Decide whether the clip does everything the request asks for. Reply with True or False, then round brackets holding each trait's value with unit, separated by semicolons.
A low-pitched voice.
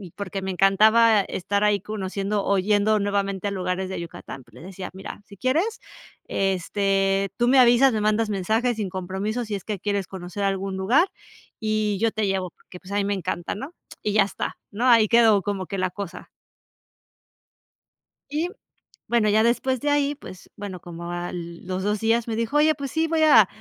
False (205 Hz)